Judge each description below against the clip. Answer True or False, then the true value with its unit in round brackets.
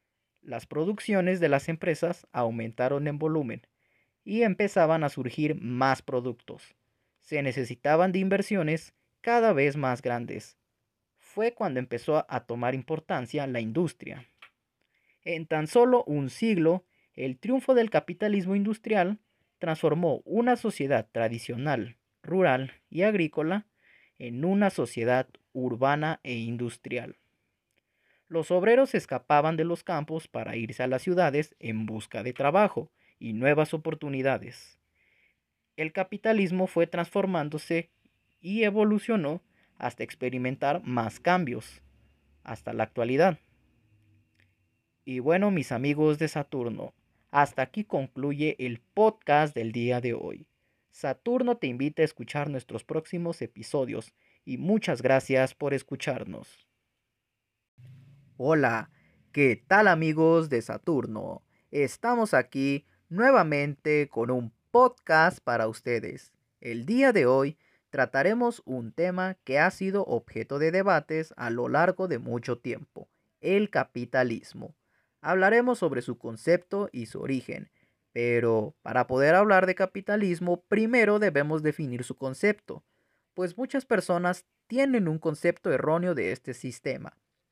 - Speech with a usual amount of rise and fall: False (6.8 semitones)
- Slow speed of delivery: True (120 wpm)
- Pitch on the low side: False (145 Hz)